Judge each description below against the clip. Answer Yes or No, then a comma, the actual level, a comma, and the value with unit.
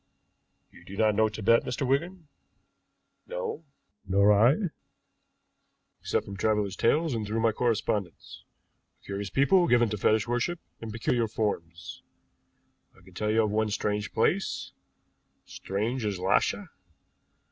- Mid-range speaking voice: No, low, 110 Hz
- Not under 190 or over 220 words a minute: No, slow, 135 wpm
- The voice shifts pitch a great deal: No, average, 3.3 semitones